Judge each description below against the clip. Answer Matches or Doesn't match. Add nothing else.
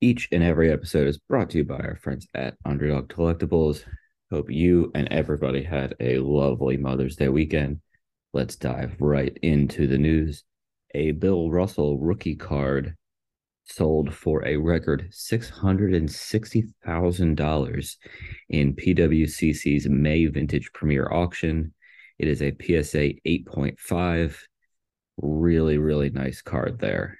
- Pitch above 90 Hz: Doesn't match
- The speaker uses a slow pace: Matches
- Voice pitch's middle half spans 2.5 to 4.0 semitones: Matches